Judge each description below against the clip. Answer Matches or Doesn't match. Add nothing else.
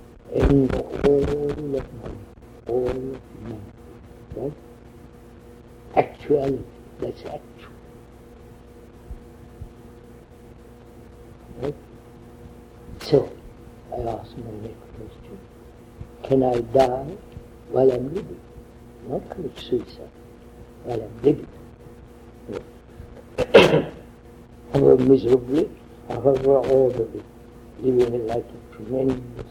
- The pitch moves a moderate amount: Doesn't match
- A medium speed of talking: Doesn't match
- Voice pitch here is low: Matches